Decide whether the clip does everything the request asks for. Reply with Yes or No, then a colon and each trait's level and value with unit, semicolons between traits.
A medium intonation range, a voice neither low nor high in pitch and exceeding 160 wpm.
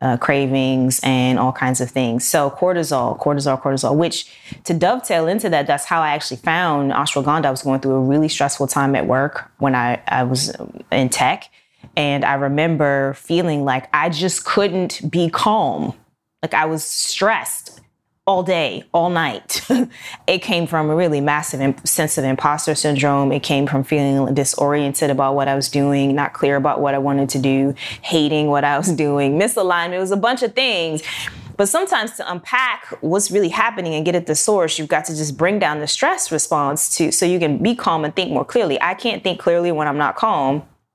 Yes: average, 3.7 semitones; medium, 150 Hz; average, 200 wpm